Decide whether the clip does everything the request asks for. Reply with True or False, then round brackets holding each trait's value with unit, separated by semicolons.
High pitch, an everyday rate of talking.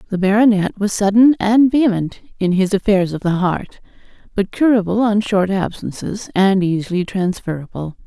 True (200 Hz; 150 wpm)